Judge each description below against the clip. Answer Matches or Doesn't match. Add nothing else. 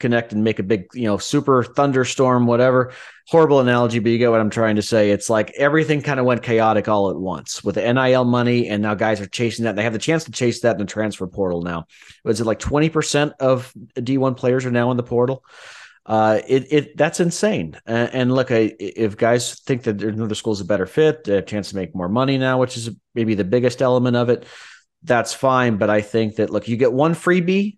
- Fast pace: Matches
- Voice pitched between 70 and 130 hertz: Matches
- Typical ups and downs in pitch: Matches